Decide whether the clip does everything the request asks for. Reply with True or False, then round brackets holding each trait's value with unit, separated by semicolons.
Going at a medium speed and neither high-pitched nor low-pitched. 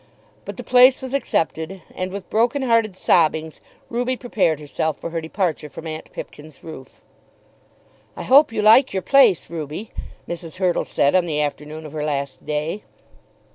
True (165 wpm; 170 Hz)